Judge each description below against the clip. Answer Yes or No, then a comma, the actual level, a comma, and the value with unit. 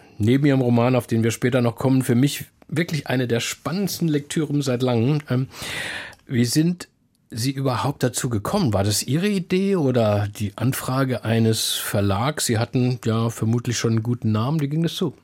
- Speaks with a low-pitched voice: Yes, low, 125 Hz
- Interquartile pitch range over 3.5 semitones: Yes, average, 4.0 semitones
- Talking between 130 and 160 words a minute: No, average, 175 wpm